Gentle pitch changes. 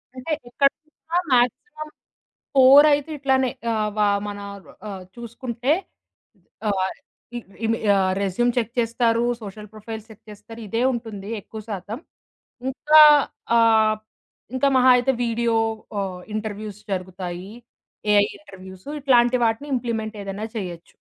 No: average, 3.8 semitones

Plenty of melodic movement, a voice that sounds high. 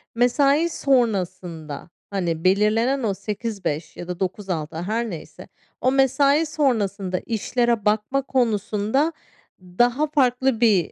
Yes: wide, 5.7 semitones; high, 220 Hz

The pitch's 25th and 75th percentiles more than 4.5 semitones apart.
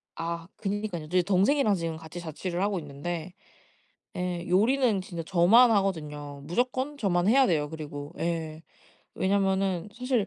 No: average, 3.9 semitones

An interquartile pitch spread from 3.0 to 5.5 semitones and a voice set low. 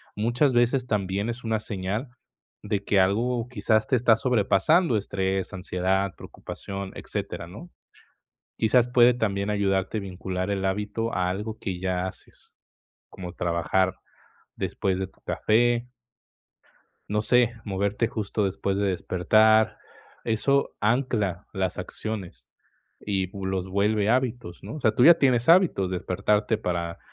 Yes: average, 3.6 semitones; low, 105 Hz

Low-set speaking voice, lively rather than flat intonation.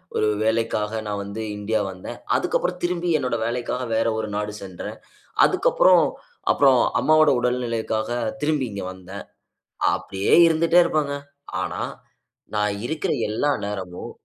Yes: low, 115 Hz; wide, 6.0 semitones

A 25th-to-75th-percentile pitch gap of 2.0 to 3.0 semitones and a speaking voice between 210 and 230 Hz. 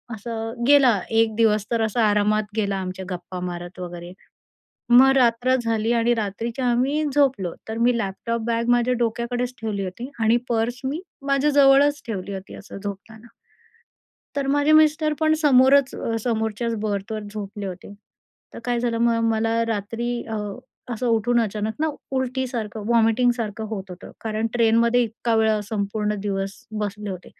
Yes: average, 2.7 semitones; high, 225 Hz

